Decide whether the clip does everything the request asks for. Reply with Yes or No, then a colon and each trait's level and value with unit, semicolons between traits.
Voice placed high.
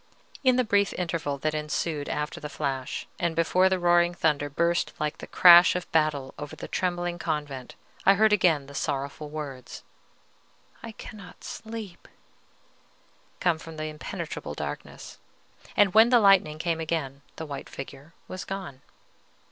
No: medium, 165 Hz